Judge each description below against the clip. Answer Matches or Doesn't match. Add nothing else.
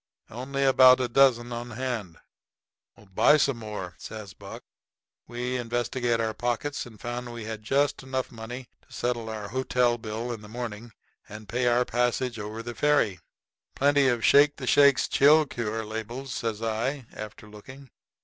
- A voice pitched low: Matches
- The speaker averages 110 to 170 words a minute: Matches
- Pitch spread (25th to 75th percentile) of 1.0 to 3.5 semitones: Matches